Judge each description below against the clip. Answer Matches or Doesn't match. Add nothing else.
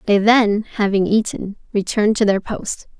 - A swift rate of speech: Doesn't match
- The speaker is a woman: Matches